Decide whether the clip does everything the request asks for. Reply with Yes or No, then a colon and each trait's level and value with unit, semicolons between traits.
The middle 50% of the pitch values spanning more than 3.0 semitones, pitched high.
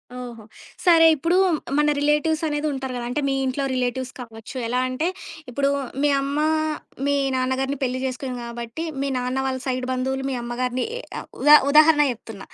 No: average, 2.7 semitones; very high, 260 Hz